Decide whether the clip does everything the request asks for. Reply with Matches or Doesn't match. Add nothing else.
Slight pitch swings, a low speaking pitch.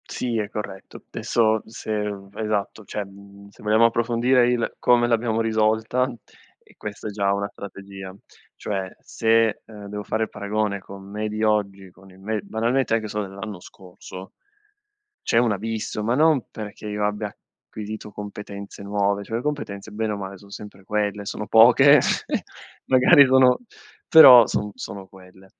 Matches